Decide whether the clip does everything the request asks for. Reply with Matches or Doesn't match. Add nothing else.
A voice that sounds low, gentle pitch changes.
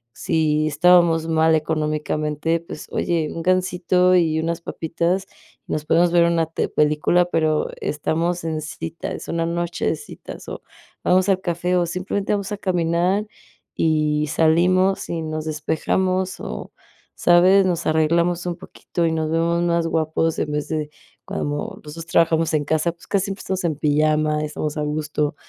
Doesn't match